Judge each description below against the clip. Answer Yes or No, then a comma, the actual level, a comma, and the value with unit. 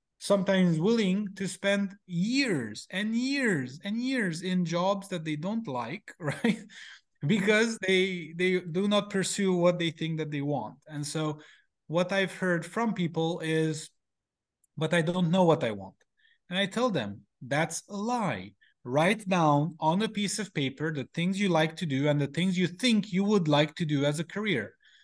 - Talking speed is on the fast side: No, average, 180 wpm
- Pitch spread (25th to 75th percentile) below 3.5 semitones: No, average, 4.3 semitones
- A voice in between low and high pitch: Yes, medium, 180 Hz